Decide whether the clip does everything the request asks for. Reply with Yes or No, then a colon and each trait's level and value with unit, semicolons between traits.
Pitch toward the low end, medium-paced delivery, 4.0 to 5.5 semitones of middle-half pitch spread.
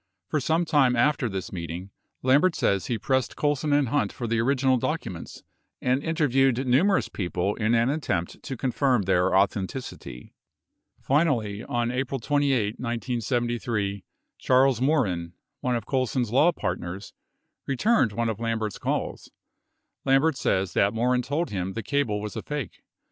Yes: low, 125 Hz; average, 150 wpm; average, 4.9 semitones